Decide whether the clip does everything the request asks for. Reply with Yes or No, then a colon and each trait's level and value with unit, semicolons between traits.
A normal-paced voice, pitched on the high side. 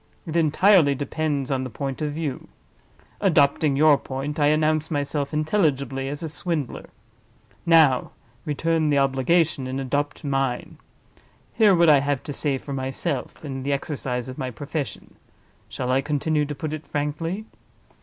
No: average, 150 wpm; medium, 145 Hz